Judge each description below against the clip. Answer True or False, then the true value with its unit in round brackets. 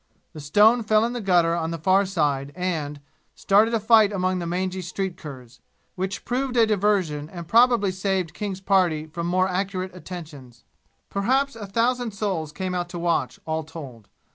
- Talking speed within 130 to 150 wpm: False (175 wpm)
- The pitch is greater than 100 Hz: True (185 Hz)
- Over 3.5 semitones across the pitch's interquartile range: True (4.1 semitones)